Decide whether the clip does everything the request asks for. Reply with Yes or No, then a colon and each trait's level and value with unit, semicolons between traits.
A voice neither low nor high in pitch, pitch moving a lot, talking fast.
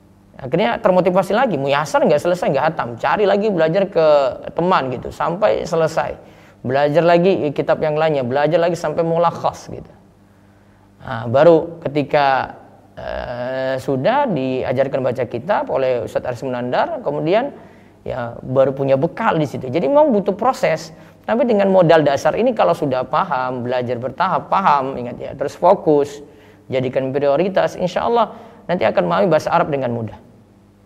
Yes: medium, 155 Hz; wide, 5.8 semitones; fast, 150 wpm